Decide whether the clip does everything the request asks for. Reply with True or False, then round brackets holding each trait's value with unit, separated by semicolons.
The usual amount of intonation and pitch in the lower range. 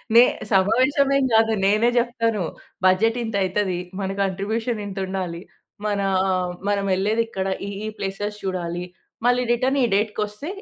False (3.0 semitones; 210 Hz)